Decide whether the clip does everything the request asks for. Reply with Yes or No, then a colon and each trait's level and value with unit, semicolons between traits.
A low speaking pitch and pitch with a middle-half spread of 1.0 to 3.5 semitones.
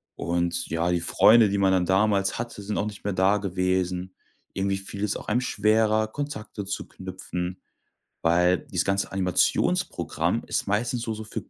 Yes: very low, 95 Hz; narrow, 2.6 semitones